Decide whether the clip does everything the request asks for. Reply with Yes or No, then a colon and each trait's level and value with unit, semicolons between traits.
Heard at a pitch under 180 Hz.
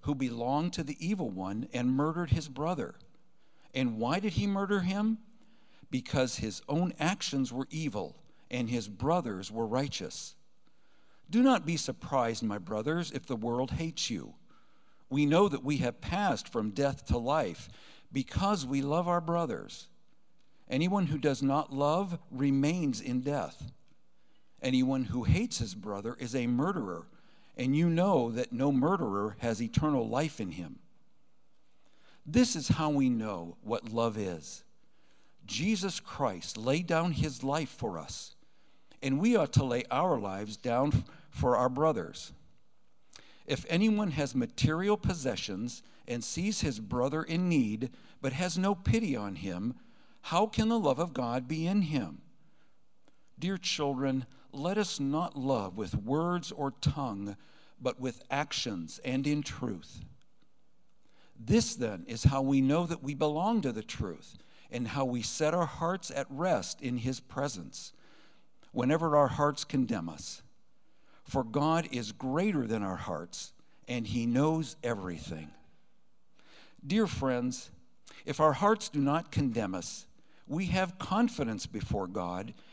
Yes: medium, 140 Hz